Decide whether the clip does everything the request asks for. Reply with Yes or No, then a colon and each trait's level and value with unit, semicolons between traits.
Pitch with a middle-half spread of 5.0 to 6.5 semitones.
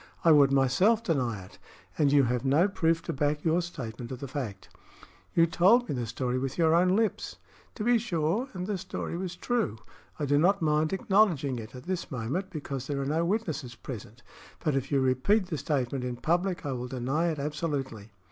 Yes: wide, 5.4 semitones